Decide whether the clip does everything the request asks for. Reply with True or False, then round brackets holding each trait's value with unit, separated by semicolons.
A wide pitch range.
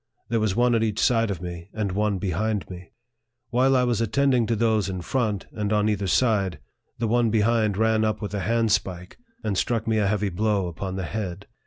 False (2.7 semitones)